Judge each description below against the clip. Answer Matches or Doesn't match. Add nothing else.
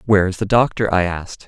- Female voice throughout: Doesn't match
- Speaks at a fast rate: Matches